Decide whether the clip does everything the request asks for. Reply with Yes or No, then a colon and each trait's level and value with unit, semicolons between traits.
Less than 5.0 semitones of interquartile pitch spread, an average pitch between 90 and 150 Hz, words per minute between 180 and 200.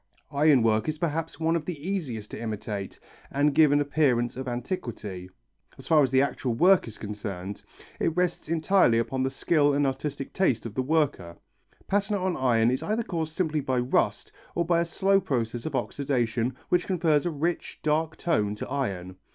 No: wide, 5.6 semitones; medium, 140 Hz; average, 185 wpm